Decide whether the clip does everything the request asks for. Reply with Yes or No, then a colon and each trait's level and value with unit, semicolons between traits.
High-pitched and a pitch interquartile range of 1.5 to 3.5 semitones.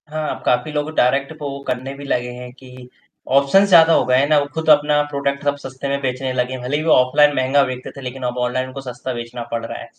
No: low, 135 Hz; narrow, 2.5 semitones